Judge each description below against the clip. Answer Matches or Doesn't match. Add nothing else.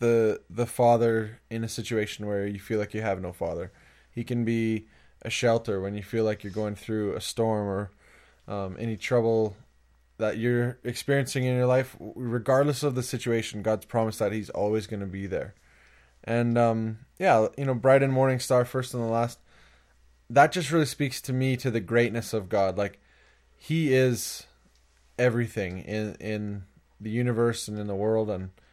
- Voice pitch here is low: Matches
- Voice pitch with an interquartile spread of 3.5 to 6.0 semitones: Doesn't match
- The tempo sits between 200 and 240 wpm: Doesn't match